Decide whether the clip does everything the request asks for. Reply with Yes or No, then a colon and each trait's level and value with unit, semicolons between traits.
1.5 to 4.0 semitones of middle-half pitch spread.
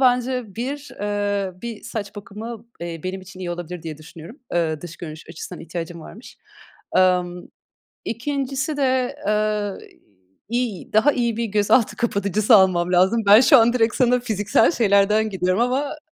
No: average, 4.7 semitones